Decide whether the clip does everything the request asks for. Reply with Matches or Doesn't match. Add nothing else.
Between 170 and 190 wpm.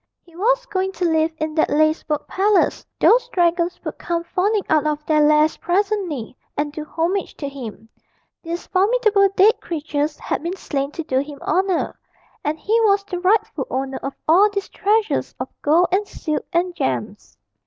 Matches